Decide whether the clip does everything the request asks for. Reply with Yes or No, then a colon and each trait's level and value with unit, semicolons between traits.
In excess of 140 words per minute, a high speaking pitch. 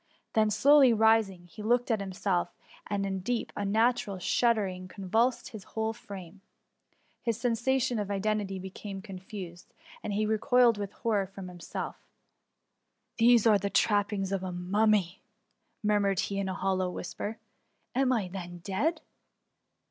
Yes: average, 150 wpm; high, 205 Hz